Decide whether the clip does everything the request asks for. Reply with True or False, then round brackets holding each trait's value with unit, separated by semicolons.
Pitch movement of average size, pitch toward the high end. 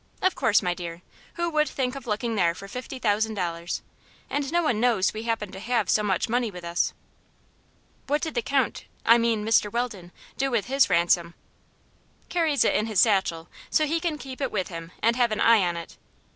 False (5.8 semitones; 225 Hz)